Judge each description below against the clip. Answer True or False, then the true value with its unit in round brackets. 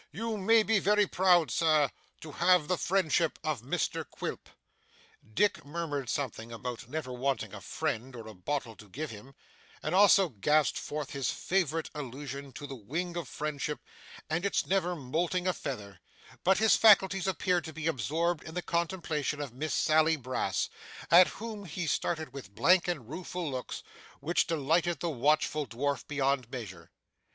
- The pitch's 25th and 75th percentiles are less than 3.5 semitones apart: False (4.8 semitones)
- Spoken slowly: False (165 wpm)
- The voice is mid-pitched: True (155 Hz)